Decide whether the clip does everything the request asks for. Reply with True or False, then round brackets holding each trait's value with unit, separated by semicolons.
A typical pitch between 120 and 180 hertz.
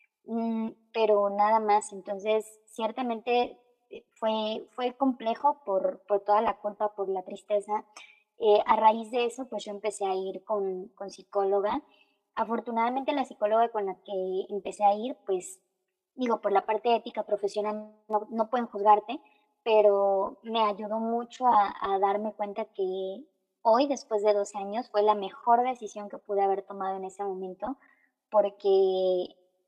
False (210 Hz)